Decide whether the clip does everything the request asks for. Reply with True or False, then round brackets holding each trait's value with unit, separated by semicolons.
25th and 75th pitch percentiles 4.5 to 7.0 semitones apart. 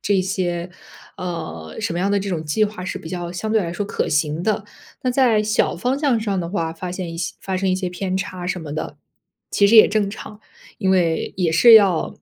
False (3.3 semitones)